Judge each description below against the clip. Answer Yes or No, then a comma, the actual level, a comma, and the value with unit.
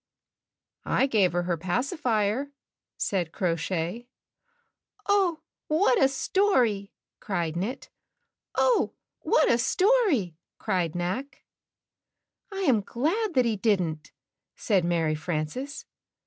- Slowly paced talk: Yes, slow, 105 wpm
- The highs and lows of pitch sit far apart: Yes, wide, 8.1 semitones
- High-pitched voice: Yes, high, 215 Hz